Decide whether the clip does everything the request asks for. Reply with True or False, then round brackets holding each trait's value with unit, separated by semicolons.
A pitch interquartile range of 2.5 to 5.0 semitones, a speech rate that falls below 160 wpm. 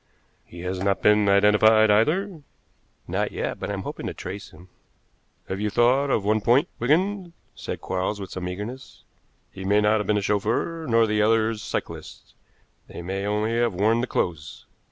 False (3.1 semitones; 175 wpm)